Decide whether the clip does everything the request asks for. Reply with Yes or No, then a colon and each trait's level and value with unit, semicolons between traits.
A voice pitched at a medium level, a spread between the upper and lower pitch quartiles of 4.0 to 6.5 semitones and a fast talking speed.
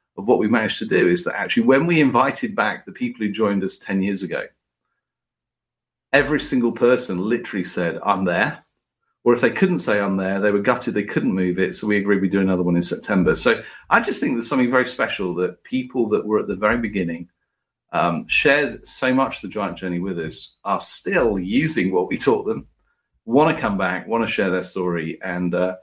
No: low, 100 Hz; average, 4.9 semitones; fast, 220 wpm